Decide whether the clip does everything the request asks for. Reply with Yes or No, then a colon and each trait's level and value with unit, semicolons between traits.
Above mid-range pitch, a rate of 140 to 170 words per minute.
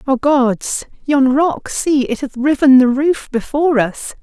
Yes: very high, 270 Hz; average, 155 wpm